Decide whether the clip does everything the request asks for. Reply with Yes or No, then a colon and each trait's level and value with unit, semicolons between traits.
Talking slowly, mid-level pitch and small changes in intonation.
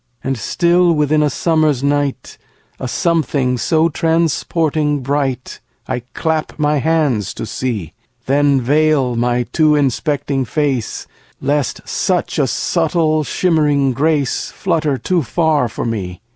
No: slow, 125 wpm; medium, 145 Hz; average, 3.5 semitones